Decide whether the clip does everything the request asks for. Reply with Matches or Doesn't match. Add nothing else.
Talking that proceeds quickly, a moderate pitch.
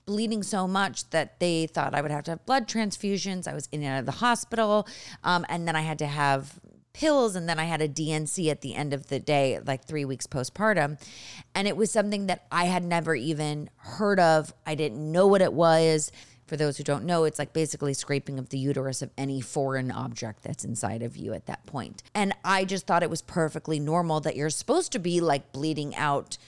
Matches